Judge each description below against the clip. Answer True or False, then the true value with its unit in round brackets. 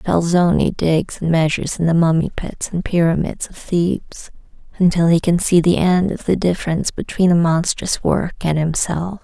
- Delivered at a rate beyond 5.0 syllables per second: False (4.9 syllables/s)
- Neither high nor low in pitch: True (170 Hz)